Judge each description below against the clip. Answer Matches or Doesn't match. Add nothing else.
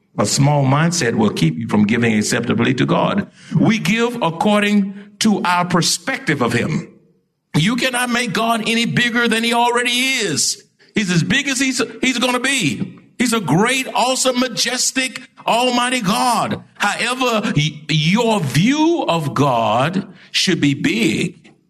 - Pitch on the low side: Doesn't match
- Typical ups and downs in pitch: Doesn't match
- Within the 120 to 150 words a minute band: Matches